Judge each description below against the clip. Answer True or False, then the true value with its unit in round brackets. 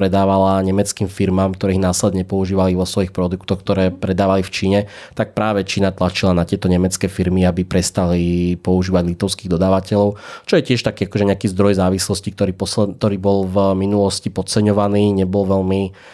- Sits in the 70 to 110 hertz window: True (95 Hz)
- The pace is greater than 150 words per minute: True (160 wpm)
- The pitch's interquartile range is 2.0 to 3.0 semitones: False (1.4 semitones)